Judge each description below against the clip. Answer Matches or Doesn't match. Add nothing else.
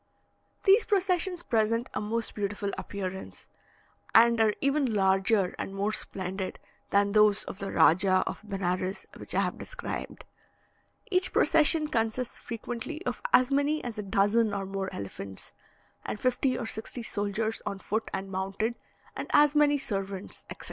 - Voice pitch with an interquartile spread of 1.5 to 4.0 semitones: Doesn't match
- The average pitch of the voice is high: Matches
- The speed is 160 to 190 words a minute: Doesn't match